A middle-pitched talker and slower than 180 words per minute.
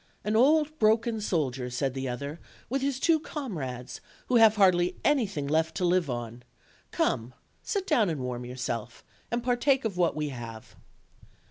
Yes: medium, 180 Hz; average, 160 wpm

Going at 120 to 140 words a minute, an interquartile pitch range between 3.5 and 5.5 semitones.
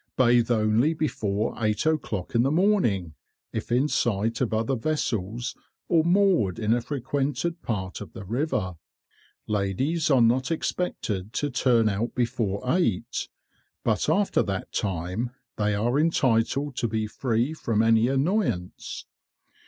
Yes: slow, 135 wpm; average, 5.0 semitones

